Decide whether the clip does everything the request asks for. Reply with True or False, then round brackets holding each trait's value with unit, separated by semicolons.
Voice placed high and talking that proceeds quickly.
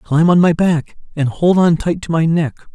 False (165 Hz; 240 wpm)